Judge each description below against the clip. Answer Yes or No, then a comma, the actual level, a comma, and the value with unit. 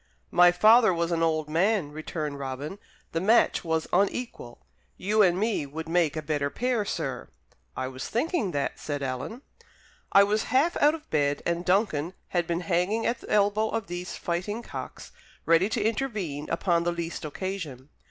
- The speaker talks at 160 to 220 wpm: Yes, average, 170 wpm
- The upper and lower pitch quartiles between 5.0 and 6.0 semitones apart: Yes, wide, 5.4 semitones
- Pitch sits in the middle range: Yes, medium, 175 Hz